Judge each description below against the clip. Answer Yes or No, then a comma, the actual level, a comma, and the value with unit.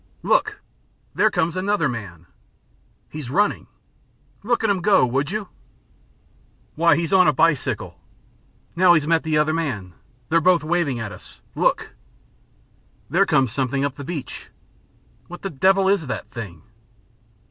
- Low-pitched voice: No, medium, 155 Hz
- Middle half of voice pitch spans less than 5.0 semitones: No, wide, 5.5 semitones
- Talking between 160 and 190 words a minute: No, average, 145 wpm